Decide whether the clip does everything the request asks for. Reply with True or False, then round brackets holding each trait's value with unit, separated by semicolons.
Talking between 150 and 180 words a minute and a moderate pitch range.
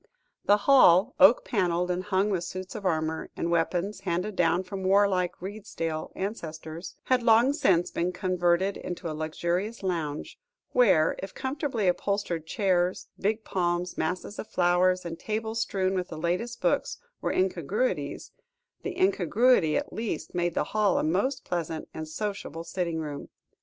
True (155 wpm; 3.6 semitones)